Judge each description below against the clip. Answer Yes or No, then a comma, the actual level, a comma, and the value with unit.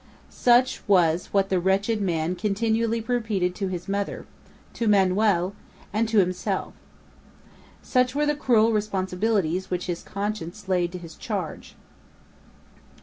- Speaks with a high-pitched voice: Yes, high, 200 Hz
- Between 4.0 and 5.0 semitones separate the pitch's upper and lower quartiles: No, average, 3.5 semitones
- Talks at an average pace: No, slow, 130 wpm